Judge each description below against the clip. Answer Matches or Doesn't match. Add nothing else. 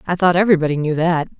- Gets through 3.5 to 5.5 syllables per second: Doesn't match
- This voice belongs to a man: Doesn't match